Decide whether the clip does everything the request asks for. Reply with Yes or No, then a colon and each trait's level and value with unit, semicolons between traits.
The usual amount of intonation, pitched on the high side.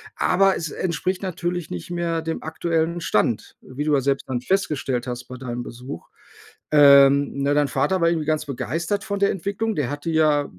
No: average, 3.9 semitones; medium, 155 Hz